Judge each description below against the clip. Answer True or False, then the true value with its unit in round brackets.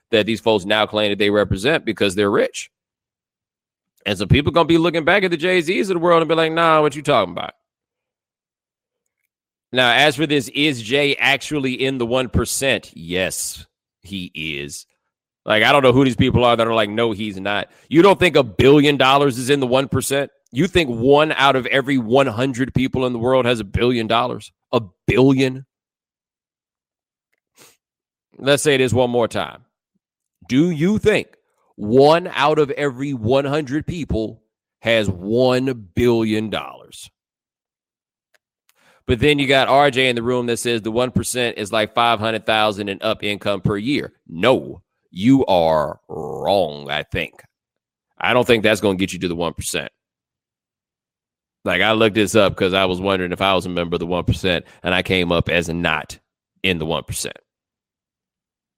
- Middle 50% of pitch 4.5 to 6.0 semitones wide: True (4.8 semitones)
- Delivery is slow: False (175 wpm)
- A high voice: False (120 Hz)